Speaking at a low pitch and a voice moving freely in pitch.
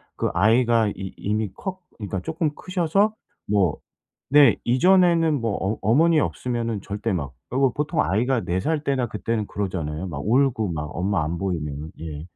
Yes: low, 110 Hz; wide, 7.1 semitones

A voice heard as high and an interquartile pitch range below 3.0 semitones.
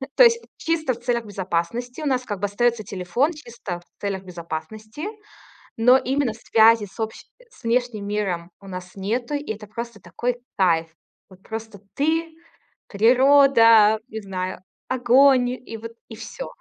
No: high, 225 Hz; average, 4.1 semitones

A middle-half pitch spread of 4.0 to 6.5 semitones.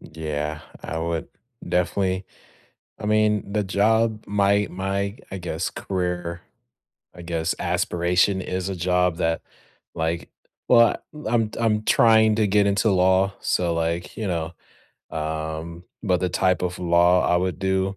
No: average, 3.0 semitones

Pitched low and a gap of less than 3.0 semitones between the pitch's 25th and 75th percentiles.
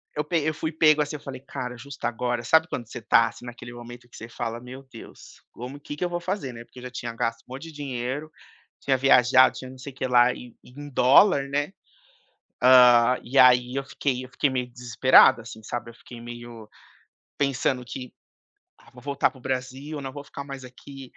Yes: low, 130 Hz; narrow, 2.4 semitones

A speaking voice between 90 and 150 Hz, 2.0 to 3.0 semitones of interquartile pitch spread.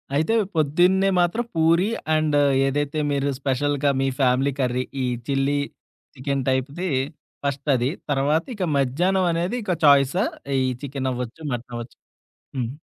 No: medium, 140 Hz; average, 3.8 semitones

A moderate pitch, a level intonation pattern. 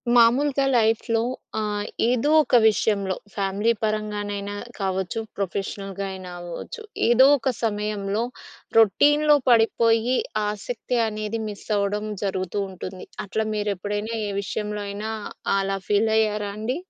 No: high, 210 Hz; narrow, 2.2 semitones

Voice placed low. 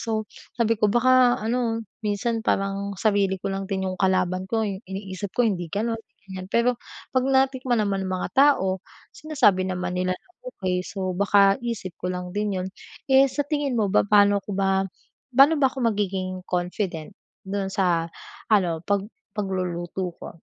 No: high, 200 Hz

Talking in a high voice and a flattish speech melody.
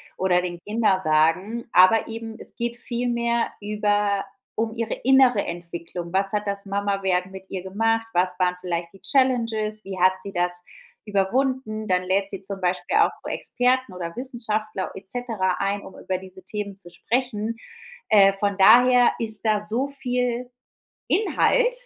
No: high, 205 Hz; average, 3.8 semitones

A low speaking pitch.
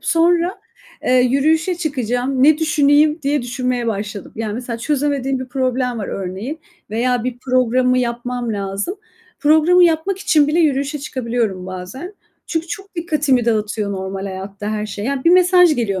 No: very high, 255 Hz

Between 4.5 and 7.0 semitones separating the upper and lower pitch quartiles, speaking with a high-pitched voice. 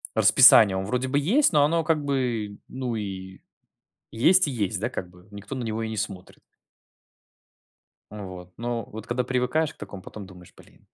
No: average, 4.8 semitones; low, 115 Hz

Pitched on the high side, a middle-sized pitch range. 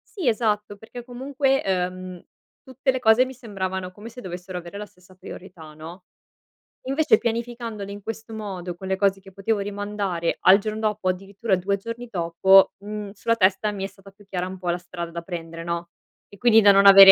Yes: high, 200 Hz; average, 3.3 semitones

